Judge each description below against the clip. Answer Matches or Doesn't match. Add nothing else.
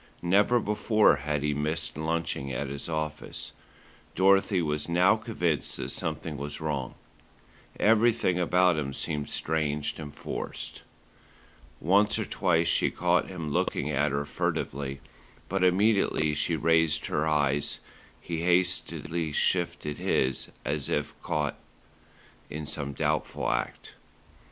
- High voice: Doesn't match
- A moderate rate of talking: Doesn't match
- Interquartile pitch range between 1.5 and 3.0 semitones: Doesn't match